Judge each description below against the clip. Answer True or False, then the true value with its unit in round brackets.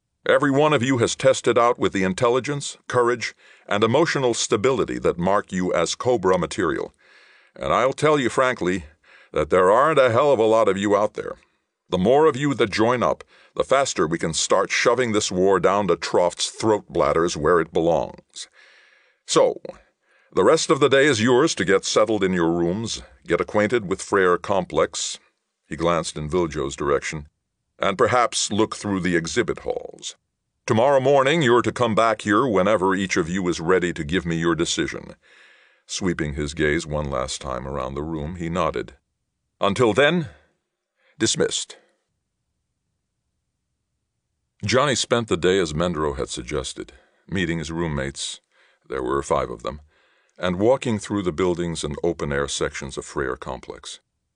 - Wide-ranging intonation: True (7.9 semitones)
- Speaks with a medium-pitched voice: False (95 Hz)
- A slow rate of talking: False (165 wpm)